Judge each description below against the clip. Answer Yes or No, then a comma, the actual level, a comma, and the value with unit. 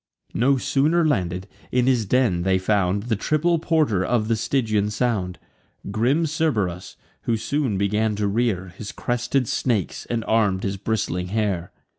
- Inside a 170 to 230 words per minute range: No, average, 150 wpm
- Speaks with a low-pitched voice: Yes, low, 110 Hz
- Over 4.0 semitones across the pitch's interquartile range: Yes, average, 4.5 semitones